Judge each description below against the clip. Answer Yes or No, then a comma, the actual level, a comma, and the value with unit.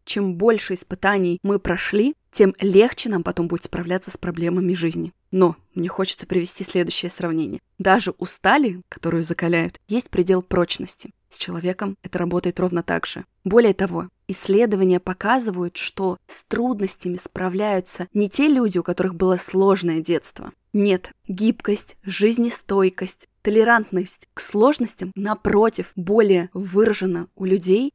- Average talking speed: Yes, average, 135 wpm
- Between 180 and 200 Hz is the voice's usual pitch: Yes, high, 190 Hz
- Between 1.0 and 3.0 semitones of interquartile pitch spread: Yes, narrow, 2.6 semitones